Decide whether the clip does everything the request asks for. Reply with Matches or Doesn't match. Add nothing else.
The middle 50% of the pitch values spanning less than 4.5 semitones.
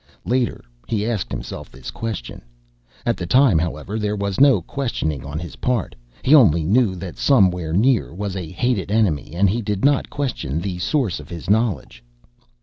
Doesn't match